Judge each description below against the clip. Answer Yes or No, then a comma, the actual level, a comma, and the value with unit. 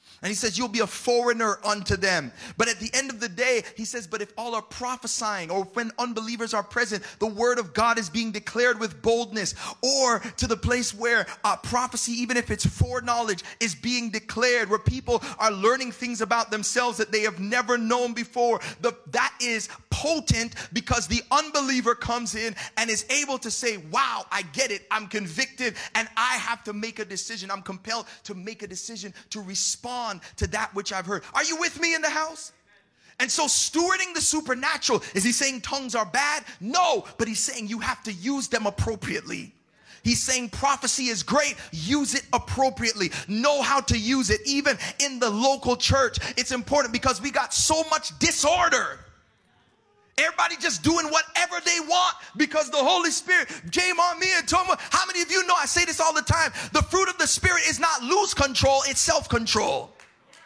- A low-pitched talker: No, high, 240 Hz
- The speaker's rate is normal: Yes, average, 195 wpm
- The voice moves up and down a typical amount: Yes, average, 4.4 semitones